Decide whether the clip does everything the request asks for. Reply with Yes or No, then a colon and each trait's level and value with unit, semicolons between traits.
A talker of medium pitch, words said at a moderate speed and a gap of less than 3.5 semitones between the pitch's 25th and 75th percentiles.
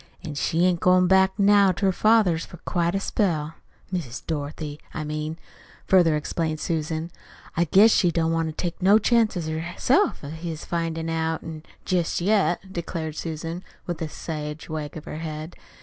Yes: medium, 165 Hz; average, 170 wpm; narrow, 2.6 semitones